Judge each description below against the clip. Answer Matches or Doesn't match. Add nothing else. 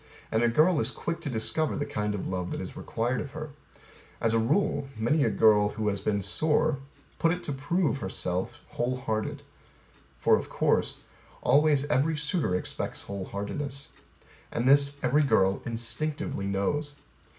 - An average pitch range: Doesn't match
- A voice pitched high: Doesn't match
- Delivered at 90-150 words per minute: Doesn't match